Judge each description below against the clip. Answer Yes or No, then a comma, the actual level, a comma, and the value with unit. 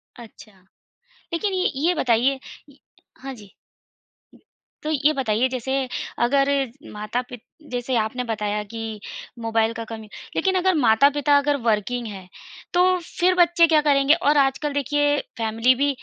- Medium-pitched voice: No, very high, 265 Hz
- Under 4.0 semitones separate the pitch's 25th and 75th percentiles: No, average, 4.6 semitones